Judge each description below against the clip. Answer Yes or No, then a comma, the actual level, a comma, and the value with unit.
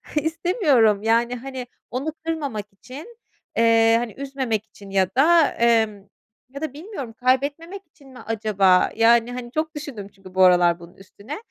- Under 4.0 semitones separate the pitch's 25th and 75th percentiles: No, wide, 5.4 semitones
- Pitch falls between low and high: No, high, 240 Hz